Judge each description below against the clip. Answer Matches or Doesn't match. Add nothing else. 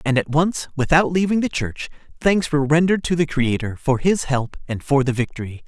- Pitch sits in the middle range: Matches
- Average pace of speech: Doesn't match